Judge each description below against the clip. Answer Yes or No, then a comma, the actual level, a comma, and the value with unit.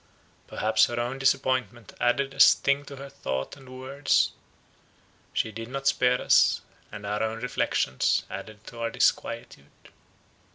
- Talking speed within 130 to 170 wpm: Yes, average, 140 wpm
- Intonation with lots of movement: No, average, 3.4 semitones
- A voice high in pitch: No, low, 120 Hz